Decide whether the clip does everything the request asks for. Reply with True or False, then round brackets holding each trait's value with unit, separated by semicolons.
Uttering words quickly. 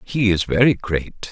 False (185 wpm)